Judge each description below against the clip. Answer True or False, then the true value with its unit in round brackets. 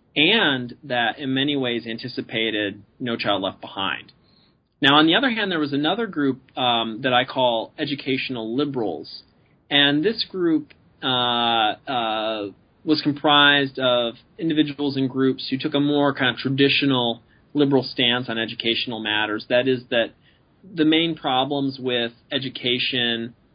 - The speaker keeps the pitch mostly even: False (3.3 semitones)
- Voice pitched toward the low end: True (130 Hz)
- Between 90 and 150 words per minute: True (145 wpm)